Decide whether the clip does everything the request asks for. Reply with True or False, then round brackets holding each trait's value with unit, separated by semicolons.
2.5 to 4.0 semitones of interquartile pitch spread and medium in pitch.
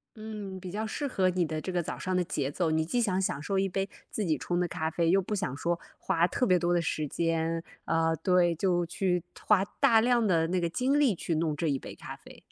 True (3.0 semitones; 180 Hz)